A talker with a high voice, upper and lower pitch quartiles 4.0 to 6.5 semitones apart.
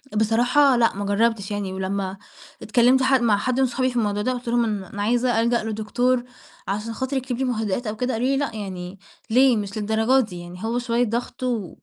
No: high, 230 Hz; average, 3.3 semitones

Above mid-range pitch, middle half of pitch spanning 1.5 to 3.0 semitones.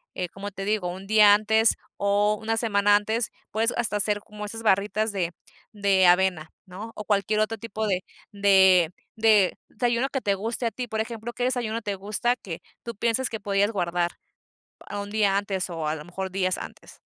Yes: high, 205 Hz; narrow, 2.5 semitones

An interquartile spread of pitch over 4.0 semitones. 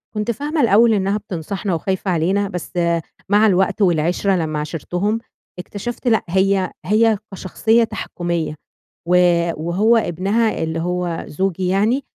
No: average, 3.7 semitones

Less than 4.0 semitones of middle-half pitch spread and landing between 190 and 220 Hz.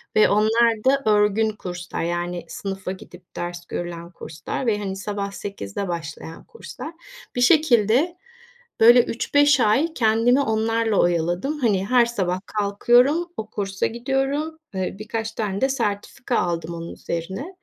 No: average, 5.1 semitones; high, 215 Hz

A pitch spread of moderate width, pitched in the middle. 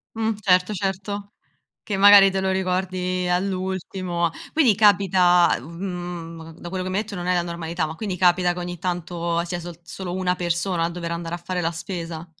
No: narrow, 1.8 semitones; medium, 180 Hz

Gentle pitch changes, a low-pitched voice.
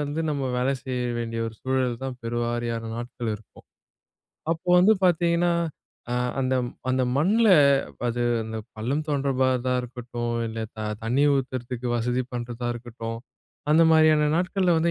No: average, 4.0 semitones; low, 125 Hz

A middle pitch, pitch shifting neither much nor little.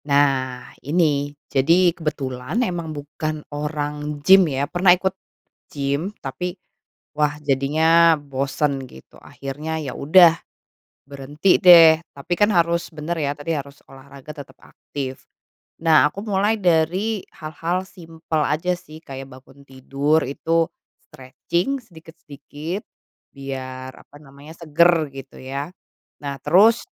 Yes: medium, 150 Hz; average, 3.4 semitones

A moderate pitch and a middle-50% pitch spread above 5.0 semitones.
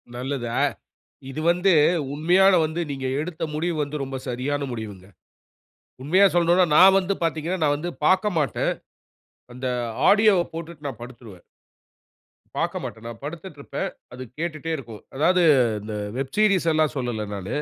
Yes: medium, 155 Hz; wide, 5.4 semitones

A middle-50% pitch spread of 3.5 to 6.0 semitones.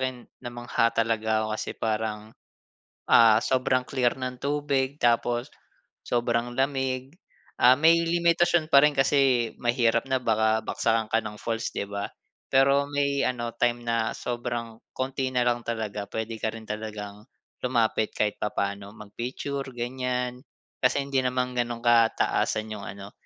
No: average, 2.8 semitones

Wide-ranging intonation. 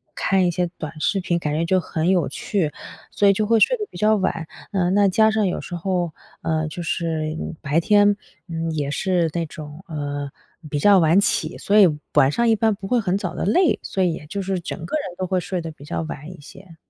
No: average, 3.8 semitones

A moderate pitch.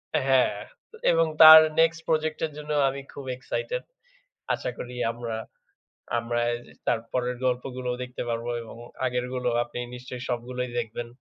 No: low, 125 Hz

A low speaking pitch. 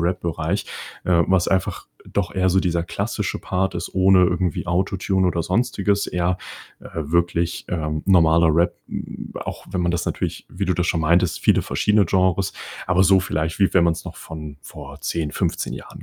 Yes: very low, 90 Hz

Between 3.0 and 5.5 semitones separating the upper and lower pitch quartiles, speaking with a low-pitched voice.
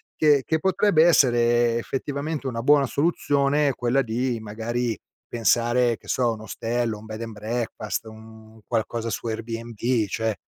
Yes: average, 3.3 semitones; low, 120 Hz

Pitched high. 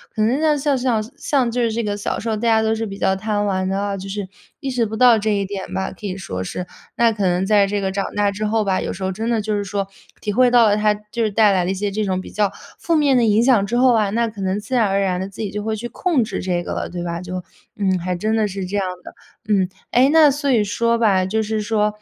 Yes: high, 210 Hz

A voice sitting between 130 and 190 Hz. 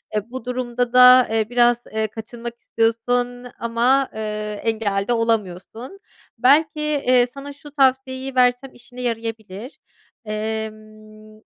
No: high, 240 Hz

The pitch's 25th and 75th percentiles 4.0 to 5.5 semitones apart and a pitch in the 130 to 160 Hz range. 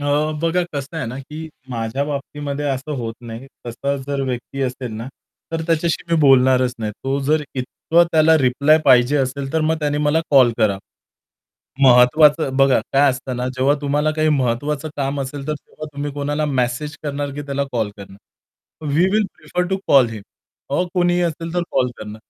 No: average, 3.2 semitones; medium, 140 Hz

